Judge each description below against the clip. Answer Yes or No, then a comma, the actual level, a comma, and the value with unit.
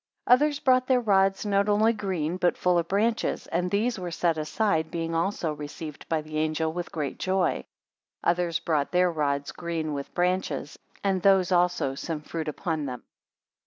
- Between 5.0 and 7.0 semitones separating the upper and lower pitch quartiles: No, average, 3.7 semitones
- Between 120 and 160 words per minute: No, average, 180 wpm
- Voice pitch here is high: No, medium, 175 Hz